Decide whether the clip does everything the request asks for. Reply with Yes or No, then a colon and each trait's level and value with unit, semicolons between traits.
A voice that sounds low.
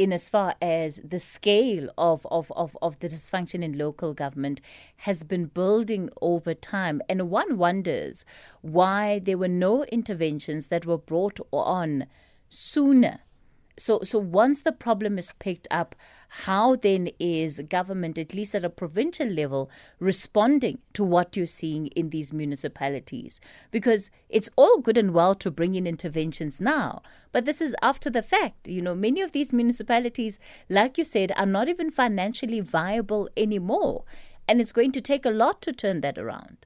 No: high, 190 Hz